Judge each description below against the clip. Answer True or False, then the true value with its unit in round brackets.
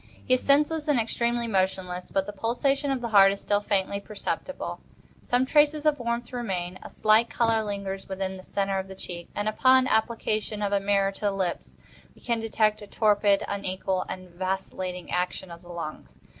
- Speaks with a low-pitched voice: False (205 Hz)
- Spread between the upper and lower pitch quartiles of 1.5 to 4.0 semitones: True (3.7 semitones)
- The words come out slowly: False (190 wpm)